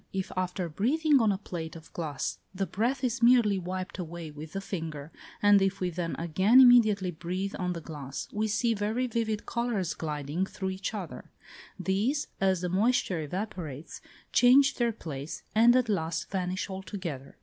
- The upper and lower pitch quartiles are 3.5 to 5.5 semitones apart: Yes, average, 4.7 semitones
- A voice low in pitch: No, high, 190 Hz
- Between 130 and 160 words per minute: No, average, 170 wpm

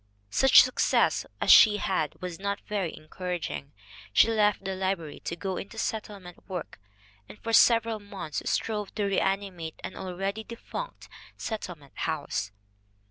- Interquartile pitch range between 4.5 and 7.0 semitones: No, average, 3.0 semitones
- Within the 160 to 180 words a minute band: No, average, 140 wpm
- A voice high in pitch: Yes, high, 195 Hz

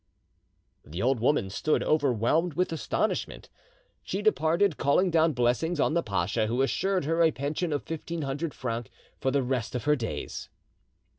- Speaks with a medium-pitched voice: Yes, medium, 145 Hz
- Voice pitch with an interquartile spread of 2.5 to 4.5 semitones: No, average, 5.0 semitones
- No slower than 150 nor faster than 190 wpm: Yes, average, 160 wpm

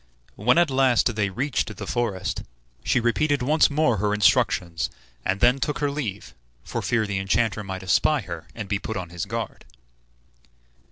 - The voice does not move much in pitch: No, average, 5.1 semitones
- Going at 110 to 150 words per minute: No, average, 170 wpm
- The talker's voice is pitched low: Yes, low, 110 Hz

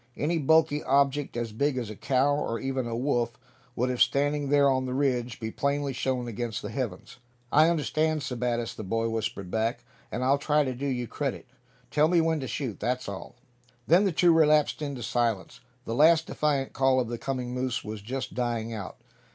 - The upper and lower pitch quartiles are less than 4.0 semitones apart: Yes, average, 3.5 semitones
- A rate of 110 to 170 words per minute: No, average, 200 wpm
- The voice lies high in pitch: No, low, 130 Hz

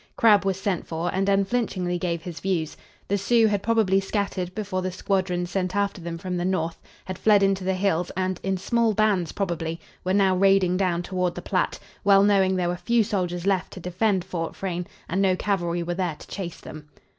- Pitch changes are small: Yes, narrow, 2.0 semitones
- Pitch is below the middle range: No, medium, 185 Hz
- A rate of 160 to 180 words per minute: No, fast, 205 wpm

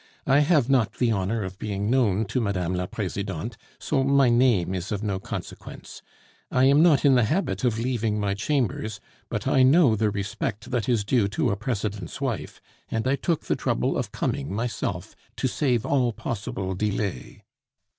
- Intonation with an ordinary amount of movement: Yes, average, 4.6 semitones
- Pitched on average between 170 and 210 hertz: No, low, 110 Hz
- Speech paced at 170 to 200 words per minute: Yes, average, 180 wpm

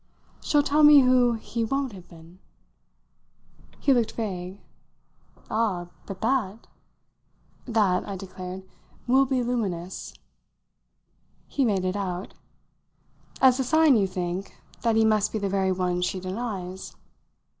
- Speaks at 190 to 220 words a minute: No, slow, 135 wpm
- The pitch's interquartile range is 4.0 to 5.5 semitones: Yes, average, 4.9 semitones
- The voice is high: Yes, high, 205 Hz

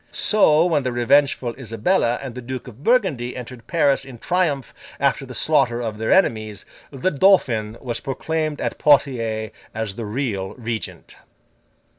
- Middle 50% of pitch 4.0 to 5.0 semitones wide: Yes, average, 4.3 semitones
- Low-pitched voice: Yes, low, 125 Hz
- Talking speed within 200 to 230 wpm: No, average, 150 wpm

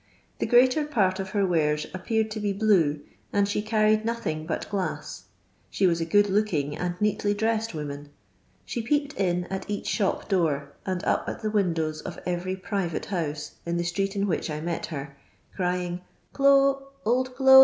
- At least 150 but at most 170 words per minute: No, average, 185 wpm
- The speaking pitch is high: Yes, high, 195 Hz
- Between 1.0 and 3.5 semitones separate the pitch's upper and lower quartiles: No, average, 4.3 semitones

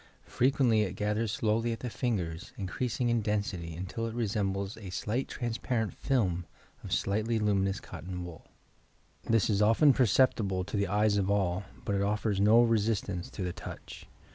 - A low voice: Yes, low, 105 Hz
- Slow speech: No, average, 165 wpm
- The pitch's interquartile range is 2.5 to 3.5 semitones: Yes, average, 3.0 semitones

